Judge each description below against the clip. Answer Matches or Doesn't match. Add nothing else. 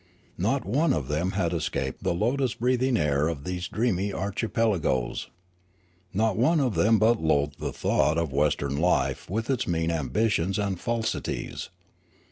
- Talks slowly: Doesn't match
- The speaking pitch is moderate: Doesn't match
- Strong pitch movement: Matches